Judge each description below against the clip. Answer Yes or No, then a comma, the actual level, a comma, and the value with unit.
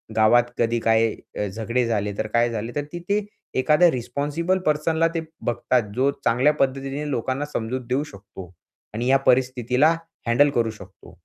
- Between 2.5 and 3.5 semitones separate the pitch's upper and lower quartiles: No, average, 4.1 semitones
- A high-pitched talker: No, low, 125 Hz